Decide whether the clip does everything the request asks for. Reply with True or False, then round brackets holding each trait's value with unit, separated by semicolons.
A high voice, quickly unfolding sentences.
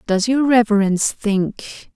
False (220 Hz; 125 wpm)